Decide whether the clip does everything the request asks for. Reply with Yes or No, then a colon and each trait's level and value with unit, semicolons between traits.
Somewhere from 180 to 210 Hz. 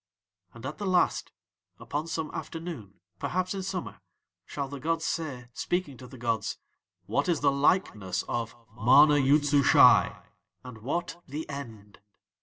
No: medium, 140 Hz